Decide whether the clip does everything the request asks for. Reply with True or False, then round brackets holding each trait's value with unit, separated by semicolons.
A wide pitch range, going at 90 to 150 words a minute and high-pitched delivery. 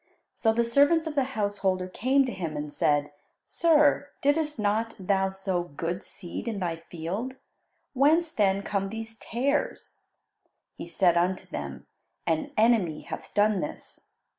True (6.6 semitones; 145 wpm; 210 Hz)